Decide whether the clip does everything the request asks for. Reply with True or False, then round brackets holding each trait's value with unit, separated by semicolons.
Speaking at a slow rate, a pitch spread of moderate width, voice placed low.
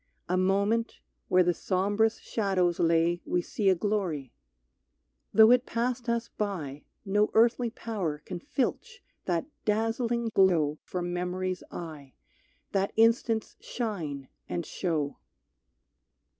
False (115 wpm; 4.6 semitones; 195 Hz)